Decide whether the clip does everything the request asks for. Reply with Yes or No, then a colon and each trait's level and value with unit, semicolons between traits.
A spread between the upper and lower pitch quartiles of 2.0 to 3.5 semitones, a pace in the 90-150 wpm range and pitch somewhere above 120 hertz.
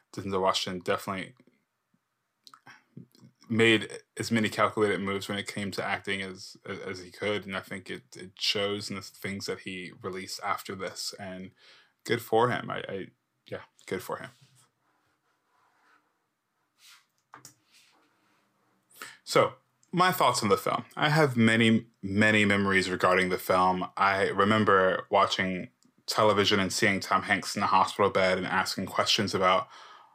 No: narrow, 2.6 semitones; average, 140 wpm; low, 100 Hz